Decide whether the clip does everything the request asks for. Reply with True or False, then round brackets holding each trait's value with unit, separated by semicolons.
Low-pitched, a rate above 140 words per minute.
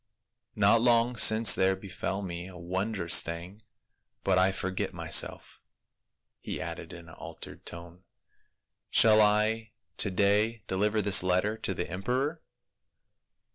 False (100 Hz; 135 wpm)